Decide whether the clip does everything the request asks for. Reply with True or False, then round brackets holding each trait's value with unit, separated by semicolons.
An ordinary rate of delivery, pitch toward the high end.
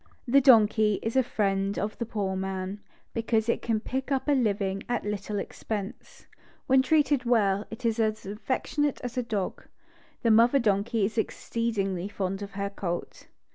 True (170 wpm; 215 Hz)